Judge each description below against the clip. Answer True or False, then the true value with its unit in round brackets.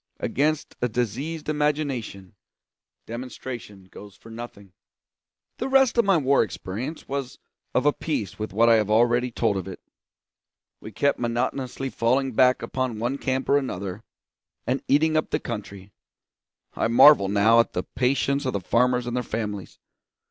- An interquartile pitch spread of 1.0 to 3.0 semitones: False (4.5 semitones)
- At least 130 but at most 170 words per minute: True (155 wpm)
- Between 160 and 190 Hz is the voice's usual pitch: False (120 Hz)